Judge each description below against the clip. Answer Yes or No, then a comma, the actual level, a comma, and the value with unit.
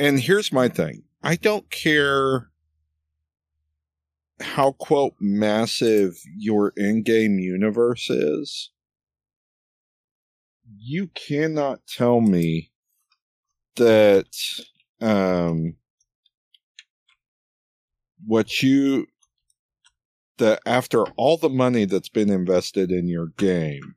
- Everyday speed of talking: No, slow, 85 wpm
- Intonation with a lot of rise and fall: Yes, wide, 8.1 semitones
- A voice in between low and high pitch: No, low, 105 Hz